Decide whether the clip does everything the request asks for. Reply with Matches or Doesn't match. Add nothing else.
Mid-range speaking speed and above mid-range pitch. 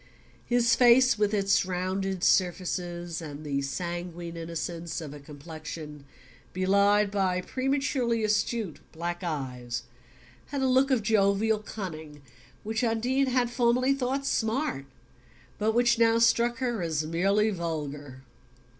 Doesn't match